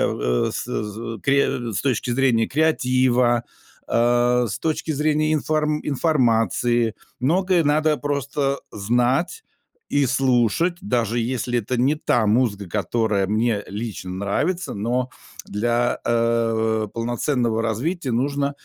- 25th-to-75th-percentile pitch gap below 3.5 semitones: No, average, 3.8 semitones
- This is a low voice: Yes, low, 120 Hz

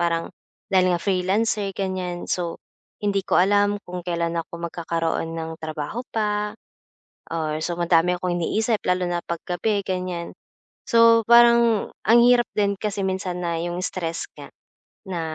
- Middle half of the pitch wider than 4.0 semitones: No, average, 3.2 semitones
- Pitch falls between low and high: Yes, medium, 180 Hz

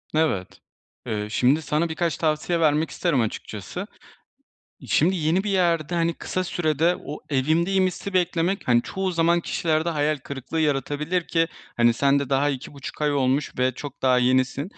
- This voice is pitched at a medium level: Yes, medium, 155 Hz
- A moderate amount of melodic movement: Yes, average, 3.8 semitones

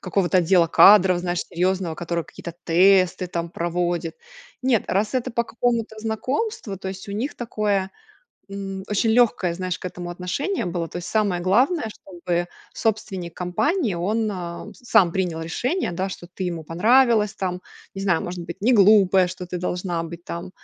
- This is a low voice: No, medium, 185 Hz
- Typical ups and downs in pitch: Yes, average, 3.7 semitones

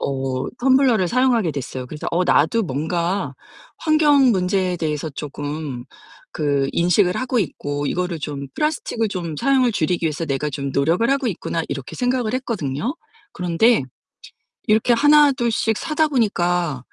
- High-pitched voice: No, medium, 180 Hz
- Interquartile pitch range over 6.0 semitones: Yes, wide, 8.5 semitones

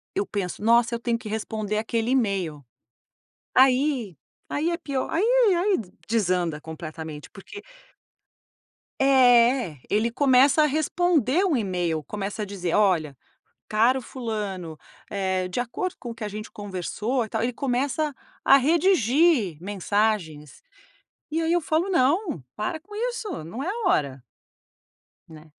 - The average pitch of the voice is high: Yes, high, 230 Hz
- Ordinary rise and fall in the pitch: No, wide, 7.1 semitones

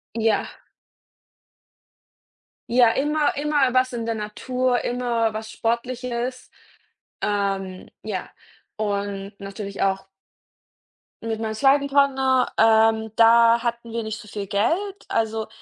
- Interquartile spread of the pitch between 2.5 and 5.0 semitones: Yes, average, 2.9 semitones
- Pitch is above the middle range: Yes, high, 230 Hz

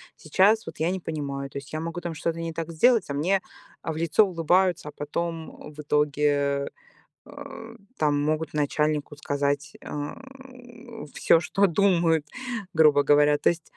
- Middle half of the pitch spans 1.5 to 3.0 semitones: Yes, narrow, 2.4 semitones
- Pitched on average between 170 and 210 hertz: No, medium, 155 Hz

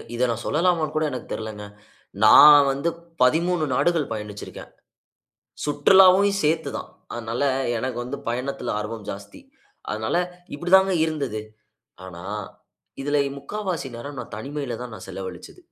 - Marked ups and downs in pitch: Yes, wide, 6.1 semitones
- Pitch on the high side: No, medium, 140 Hz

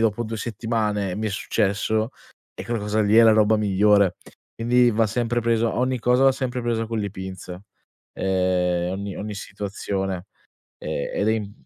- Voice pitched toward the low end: Yes, low, 105 Hz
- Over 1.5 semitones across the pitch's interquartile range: Yes, average, 2.7 semitones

